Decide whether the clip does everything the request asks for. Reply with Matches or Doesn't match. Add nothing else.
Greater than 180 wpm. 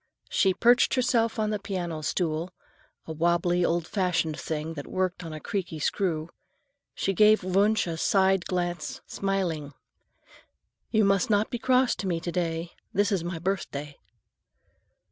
Doesn't match